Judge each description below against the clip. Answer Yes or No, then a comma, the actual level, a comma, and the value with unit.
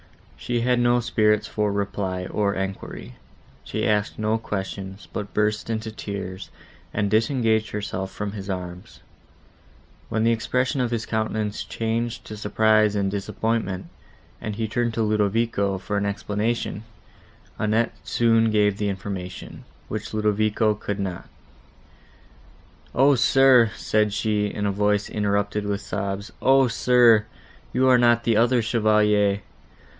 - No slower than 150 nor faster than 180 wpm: No, slow, 135 wpm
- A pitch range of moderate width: No, narrow, 2.0 semitones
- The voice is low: Yes, low, 105 Hz